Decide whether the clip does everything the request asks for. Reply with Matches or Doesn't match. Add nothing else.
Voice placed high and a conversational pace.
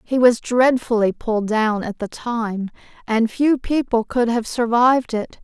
Matches